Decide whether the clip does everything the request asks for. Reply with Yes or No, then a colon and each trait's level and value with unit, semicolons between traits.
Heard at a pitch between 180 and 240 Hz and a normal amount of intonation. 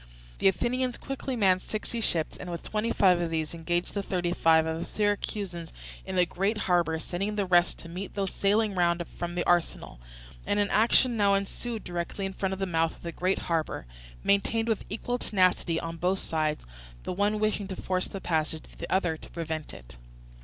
Yes: medium, 185 Hz; average, 3.3 semitones